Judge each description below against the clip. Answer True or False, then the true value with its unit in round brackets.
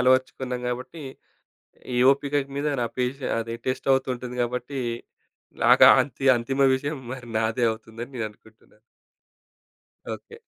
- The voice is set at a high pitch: False (125 Hz)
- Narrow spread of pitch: True (2.3 semitones)